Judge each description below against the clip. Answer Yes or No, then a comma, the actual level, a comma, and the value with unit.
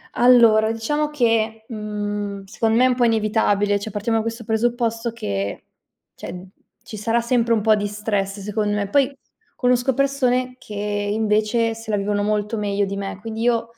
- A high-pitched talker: Yes, high, 220 Hz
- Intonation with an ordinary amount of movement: No, narrow, 2.2 semitones